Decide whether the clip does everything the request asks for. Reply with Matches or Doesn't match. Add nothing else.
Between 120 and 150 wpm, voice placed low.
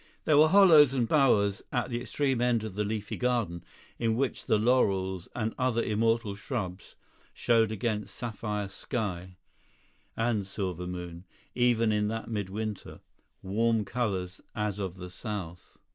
Matches